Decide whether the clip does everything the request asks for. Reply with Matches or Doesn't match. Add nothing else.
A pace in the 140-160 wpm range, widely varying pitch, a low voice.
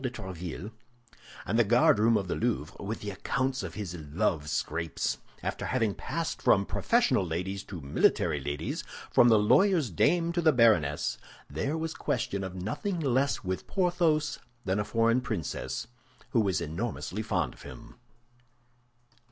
Matches